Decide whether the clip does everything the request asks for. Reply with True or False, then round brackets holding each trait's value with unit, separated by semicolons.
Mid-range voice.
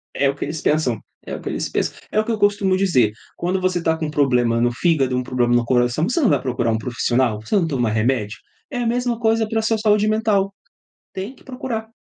True (160 Hz)